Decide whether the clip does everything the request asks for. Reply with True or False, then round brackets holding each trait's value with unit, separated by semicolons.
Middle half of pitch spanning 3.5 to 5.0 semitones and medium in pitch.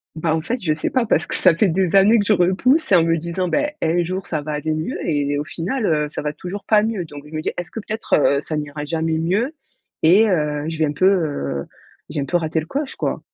True (4.2 semitones; 165 Hz)